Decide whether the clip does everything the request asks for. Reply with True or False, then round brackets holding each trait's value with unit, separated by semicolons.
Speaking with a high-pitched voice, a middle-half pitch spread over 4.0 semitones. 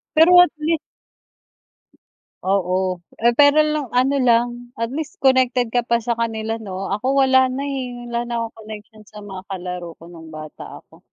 True (235 Hz; 4.4 semitones)